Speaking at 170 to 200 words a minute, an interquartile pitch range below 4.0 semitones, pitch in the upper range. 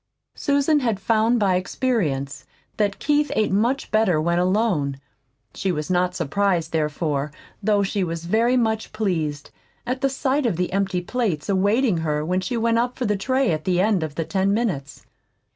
No: average, 175 wpm; wide, 5.5 semitones; high, 195 Hz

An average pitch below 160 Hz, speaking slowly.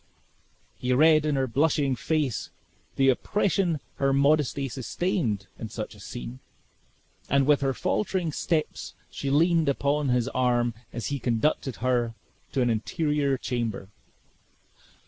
Yes: low, 135 Hz; slow, 130 wpm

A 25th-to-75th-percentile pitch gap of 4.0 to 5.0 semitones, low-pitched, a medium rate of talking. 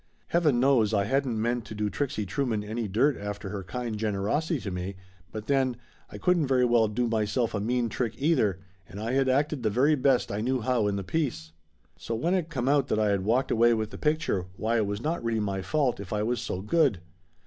No: average, 4.4 semitones; low, 115 Hz; fast, 235 wpm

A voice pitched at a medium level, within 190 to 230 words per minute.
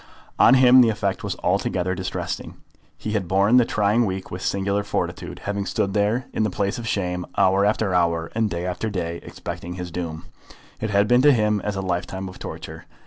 No: low, 100 Hz; average, 200 wpm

